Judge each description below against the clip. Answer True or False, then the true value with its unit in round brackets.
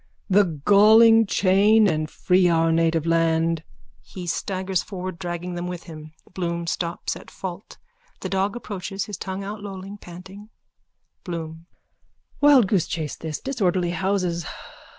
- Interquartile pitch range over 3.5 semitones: False (3.0 semitones)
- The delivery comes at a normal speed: False (130 wpm)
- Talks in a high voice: False (180 Hz)